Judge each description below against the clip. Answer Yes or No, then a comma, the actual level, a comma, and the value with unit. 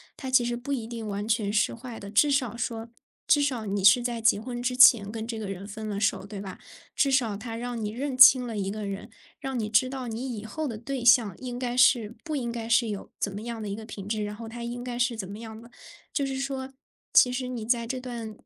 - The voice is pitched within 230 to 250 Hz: Yes, high, 235 Hz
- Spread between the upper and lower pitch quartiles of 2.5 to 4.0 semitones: Yes, average, 2.8 semitones